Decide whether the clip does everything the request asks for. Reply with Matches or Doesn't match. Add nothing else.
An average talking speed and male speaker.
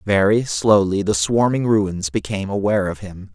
Matches